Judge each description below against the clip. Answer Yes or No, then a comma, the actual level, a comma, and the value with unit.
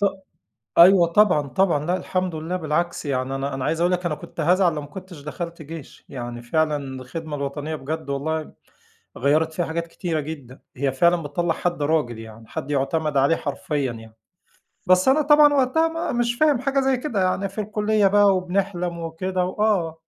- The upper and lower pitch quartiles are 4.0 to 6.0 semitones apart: Yes, average, 4.6 semitones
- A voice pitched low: No, medium, 165 Hz